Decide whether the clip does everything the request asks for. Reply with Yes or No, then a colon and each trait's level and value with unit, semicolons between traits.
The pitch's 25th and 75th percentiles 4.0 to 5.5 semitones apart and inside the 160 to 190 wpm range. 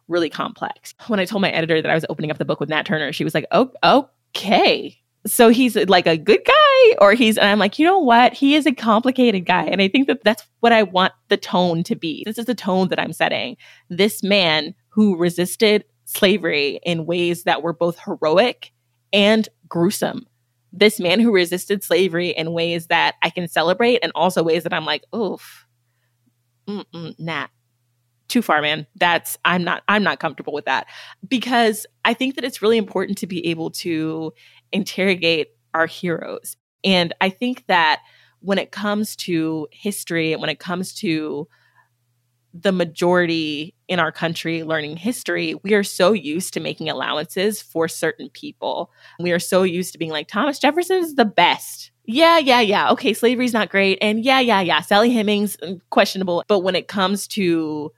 Yes: average, 4.6 semitones; average, 185 wpm